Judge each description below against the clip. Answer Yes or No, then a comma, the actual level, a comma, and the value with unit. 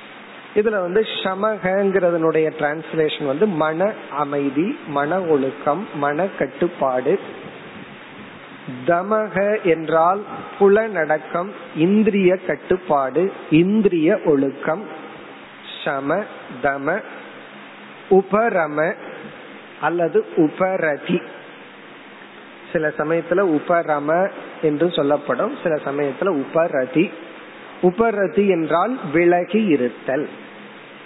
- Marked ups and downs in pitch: No, average, 4.8 semitones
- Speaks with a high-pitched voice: No, medium, 165 Hz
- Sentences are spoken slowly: Yes, slow, 70 wpm